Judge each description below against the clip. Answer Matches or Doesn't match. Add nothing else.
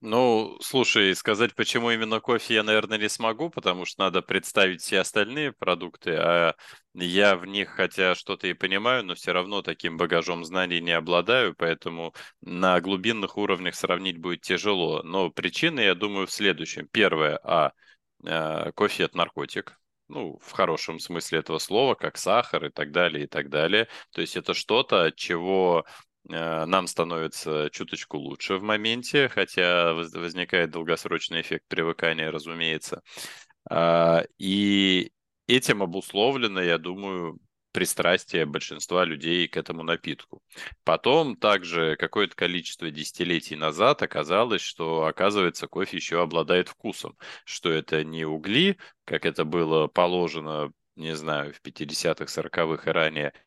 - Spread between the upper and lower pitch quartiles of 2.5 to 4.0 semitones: Matches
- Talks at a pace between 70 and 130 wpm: Doesn't match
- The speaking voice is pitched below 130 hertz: Matches